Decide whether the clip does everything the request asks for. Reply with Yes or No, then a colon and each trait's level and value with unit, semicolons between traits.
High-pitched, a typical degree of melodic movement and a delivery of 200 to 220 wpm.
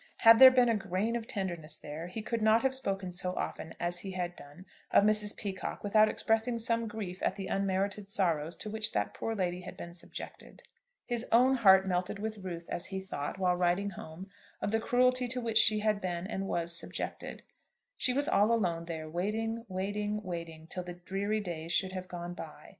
Yes: high, 195 Hz; average, 3.8 semitones; fast, 205 wpm